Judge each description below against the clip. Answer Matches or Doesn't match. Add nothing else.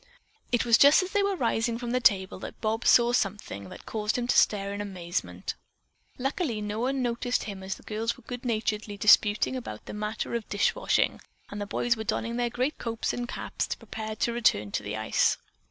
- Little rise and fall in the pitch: Doesn't match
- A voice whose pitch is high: Matches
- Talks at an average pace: Doesn't match